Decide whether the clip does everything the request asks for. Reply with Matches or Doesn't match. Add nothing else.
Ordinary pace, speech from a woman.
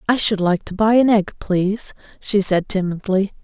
Matches